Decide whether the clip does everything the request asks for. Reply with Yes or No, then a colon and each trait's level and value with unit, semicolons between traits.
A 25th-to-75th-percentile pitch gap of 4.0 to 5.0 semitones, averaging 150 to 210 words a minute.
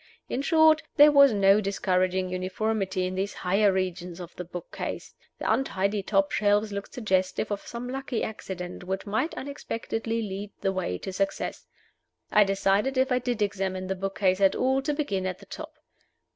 No: average, 3.6 semitones; average, 180 wpm